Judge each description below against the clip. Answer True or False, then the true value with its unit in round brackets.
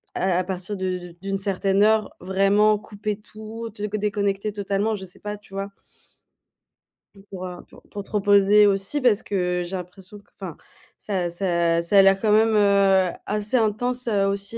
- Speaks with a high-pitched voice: True (200 Hz)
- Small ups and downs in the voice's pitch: True (1.7 semitones)